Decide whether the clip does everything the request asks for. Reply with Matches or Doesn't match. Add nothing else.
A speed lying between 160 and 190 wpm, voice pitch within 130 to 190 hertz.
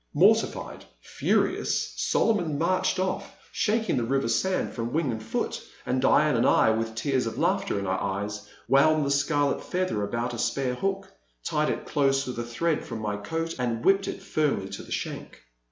Matches